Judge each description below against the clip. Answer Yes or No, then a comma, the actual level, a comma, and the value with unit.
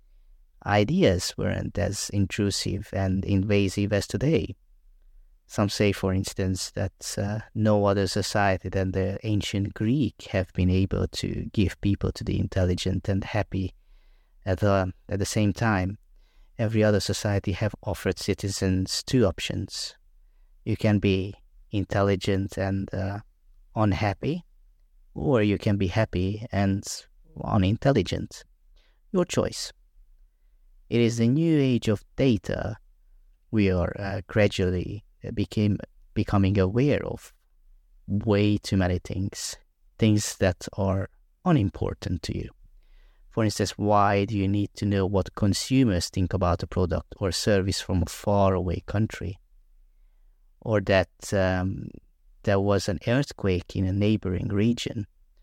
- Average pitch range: No, narrow, 1.9 semitones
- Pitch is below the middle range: Yes, low, 100 Hz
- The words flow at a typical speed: No, slow, 130 wpm